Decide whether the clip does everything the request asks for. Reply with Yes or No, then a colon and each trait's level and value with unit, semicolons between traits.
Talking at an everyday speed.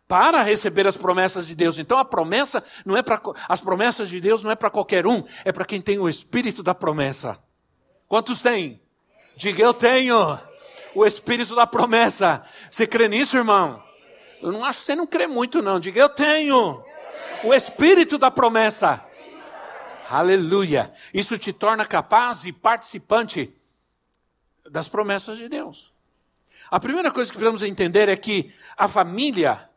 Yes: average, 160 wpm